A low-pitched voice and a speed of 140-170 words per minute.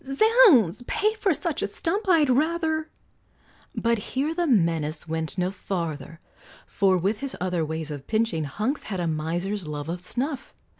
No: high, 205 Hz; average, 165 wpm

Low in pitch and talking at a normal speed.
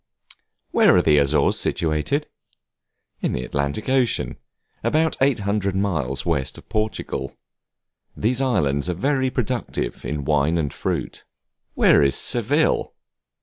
No: very low, 95 Hz; slow, 120 wpm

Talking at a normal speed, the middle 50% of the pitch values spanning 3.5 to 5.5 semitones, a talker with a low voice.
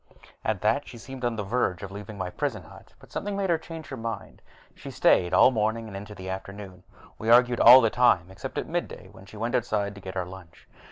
No: fast, 240 wpm; average, 4.1 semitones; low, 110 Hz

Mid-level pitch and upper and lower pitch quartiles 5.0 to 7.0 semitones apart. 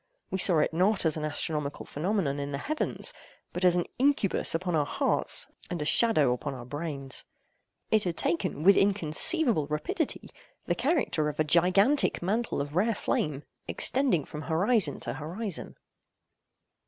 Yes: medium, 170 Hz; wide, 5.5 semitones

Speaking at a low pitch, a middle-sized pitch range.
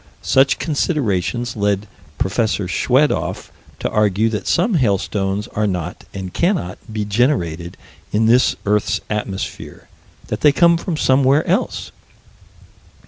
No: low, 110 Hz; wide, 6.1 semitones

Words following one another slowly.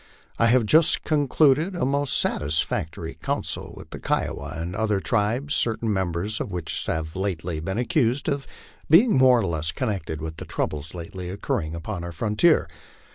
No: average, 165 wpm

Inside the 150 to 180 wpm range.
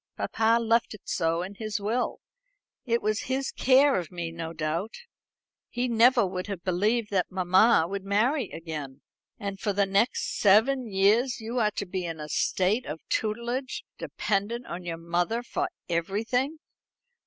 Yes: average, 160 wpm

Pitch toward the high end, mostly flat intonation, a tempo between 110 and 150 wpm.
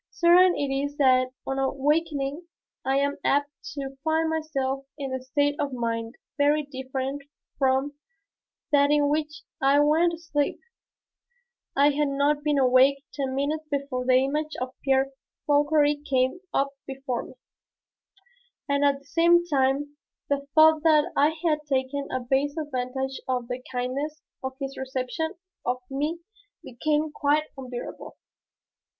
Yes: very high, 280 Hz; narrow, 2.1 semitones; average, 145 wpm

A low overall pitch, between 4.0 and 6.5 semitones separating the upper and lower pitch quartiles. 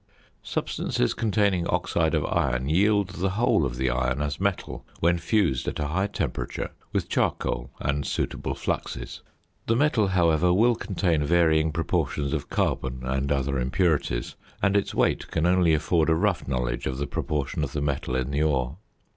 Yes: very low, 80 Hz; wide, 5.4 semitones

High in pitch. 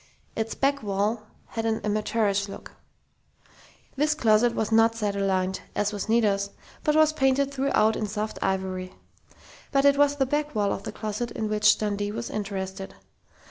Yes: high, 215 Hz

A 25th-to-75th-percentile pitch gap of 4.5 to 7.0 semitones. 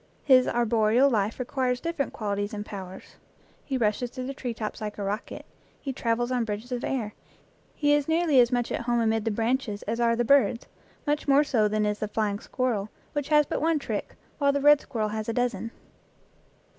No: average, 4.0 semitones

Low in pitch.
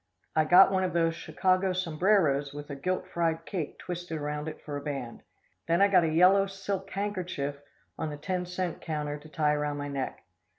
No: medium, 165 Hz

